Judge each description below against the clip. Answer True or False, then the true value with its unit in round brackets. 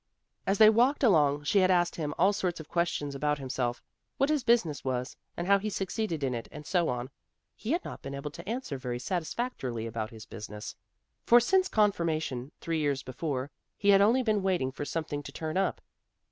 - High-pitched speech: False (160 Hz)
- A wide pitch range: True (7.0 semitones)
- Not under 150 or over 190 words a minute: False (200 wpm)